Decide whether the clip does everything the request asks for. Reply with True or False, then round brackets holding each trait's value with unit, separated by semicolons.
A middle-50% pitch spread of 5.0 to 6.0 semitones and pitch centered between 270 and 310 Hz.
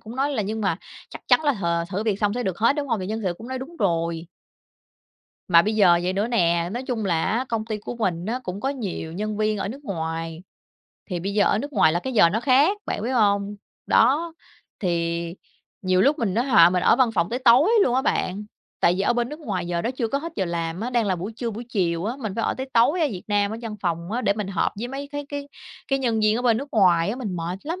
False (5.5 semitones; 215 Hz)